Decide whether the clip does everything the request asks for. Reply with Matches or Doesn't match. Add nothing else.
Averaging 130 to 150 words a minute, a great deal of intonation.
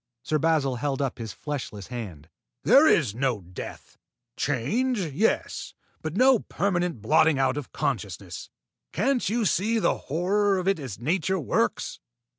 Matches